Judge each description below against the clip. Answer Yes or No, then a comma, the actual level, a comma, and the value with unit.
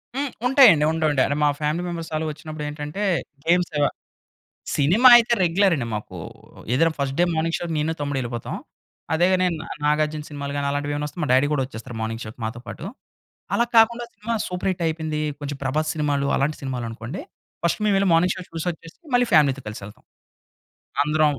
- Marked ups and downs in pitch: No, average, 3.7 semitones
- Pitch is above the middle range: No, medium, 155 Hz